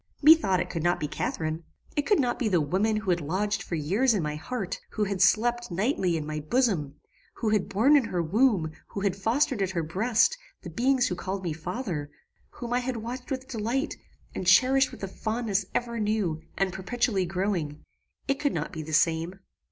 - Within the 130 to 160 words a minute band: No, fast, 205 wpm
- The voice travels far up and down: Yes, wide, 5.8 semitones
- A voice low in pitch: No, high, 200 Hz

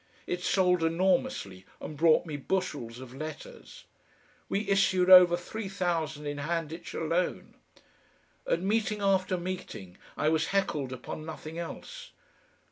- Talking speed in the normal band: No, slow, 125 wpm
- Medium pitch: Yes, medium, 170 Hz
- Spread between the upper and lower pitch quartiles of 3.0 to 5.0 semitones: Yes, average, 3.7 semitones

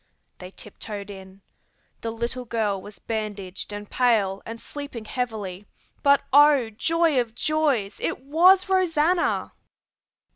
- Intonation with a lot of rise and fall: Yes, wide, 6.0 semitones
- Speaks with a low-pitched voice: No, high, 230 Hz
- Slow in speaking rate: Yes, slow, 120 wpm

